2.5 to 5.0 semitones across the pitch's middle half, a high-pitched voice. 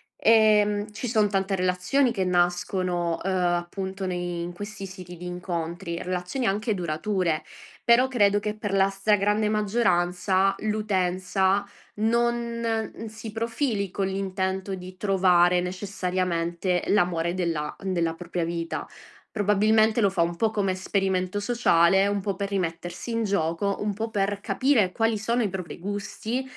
Yes: average, 2.9 semitones; high, 195 Hz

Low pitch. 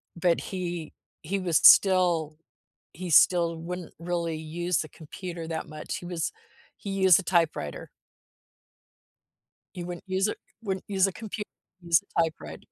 No: medium, 175 Hz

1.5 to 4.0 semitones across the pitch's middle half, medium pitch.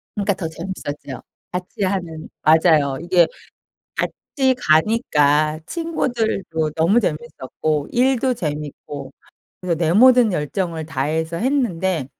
No: average, 5.3 semitones; medium, 165 Hz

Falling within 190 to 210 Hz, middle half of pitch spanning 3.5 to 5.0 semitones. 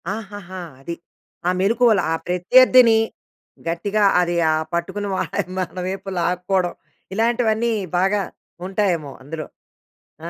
Yes: high, 195 Hz; average, 3.8 semitones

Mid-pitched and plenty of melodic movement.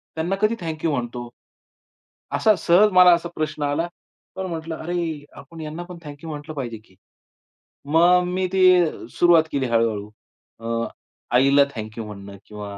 Yes: medium, 155 Hz; wide, 6.0 semitones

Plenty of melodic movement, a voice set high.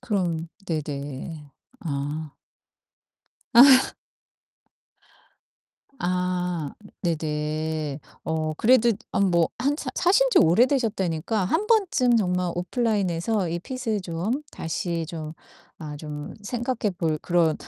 No: wide, 6.3 semitones; medium, 175 Hz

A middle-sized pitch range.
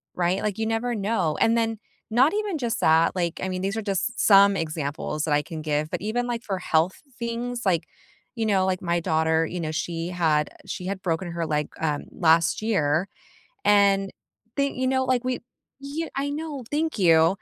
No: wide, 6.2 semitones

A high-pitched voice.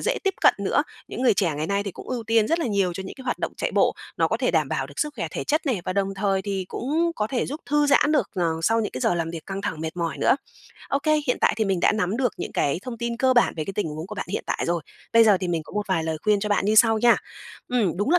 Yes: high, 210 Hz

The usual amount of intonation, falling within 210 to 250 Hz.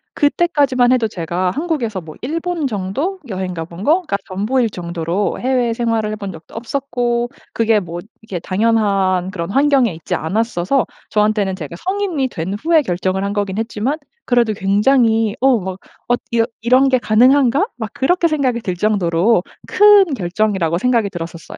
No: wide, 5.7 semitones; high, 225 Hz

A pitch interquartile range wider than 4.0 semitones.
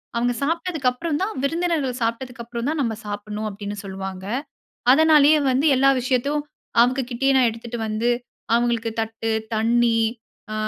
No: average, 3.7 semitones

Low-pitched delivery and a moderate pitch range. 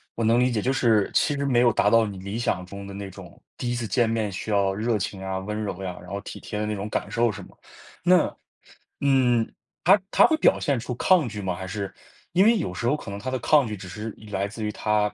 Yes: low, 105 Hz; average, 3.6 semitones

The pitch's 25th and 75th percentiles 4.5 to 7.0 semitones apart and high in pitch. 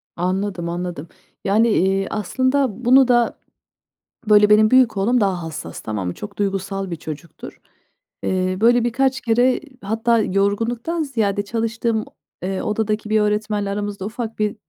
No: average, 3.3 semitones; high, 210 Hz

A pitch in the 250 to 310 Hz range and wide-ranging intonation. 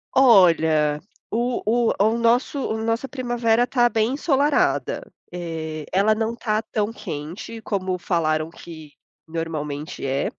No: high, 215 Hz; wide, 6.6 semitones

